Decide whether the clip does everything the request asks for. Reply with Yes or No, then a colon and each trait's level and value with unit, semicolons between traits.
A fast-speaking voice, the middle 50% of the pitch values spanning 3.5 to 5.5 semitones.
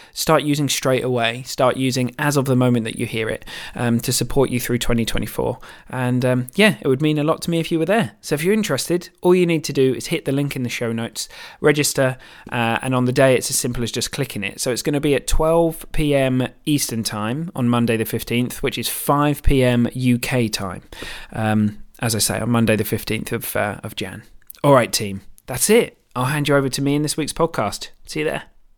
Yes: fast, 240 wpm; average, 3.9 semitones